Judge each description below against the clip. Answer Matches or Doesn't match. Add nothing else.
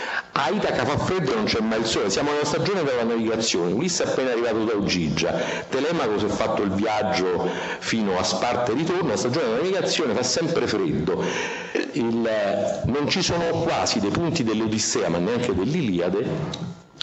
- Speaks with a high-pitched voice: Doesn't match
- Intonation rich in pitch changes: Matches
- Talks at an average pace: Doesn't match